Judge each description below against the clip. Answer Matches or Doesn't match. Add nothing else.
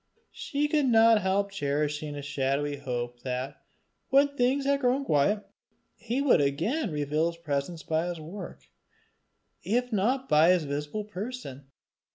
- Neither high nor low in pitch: Matches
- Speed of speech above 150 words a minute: Doesn't match